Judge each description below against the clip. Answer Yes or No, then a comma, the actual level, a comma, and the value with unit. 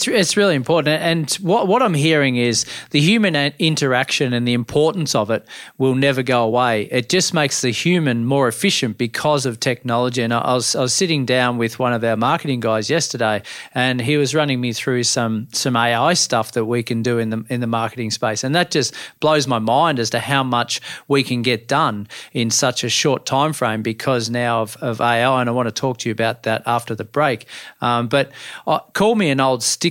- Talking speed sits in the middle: No, fast, 215 wpm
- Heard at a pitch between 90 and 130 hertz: Yes, low, 125 Hz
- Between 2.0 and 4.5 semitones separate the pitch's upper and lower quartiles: Yes, average, 3.9 semitones